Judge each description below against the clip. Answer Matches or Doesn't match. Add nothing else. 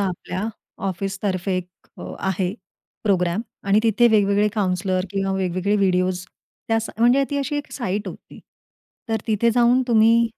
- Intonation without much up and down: Doesn't match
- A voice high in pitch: Matches